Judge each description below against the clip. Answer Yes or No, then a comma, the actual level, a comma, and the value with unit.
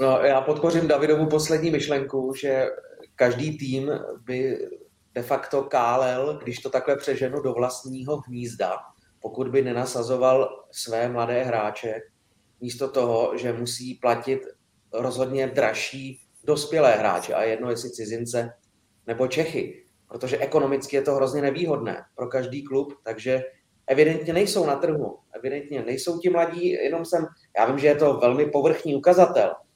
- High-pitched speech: No, low, 135 Hz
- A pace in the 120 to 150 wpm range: Yes, average, 140 wpm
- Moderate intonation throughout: Yes, average, 3.6 semitones